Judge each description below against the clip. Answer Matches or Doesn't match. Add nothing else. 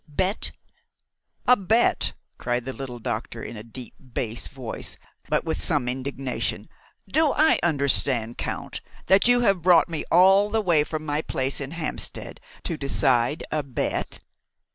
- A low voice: Doesn't match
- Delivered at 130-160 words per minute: Matches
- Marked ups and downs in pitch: Matches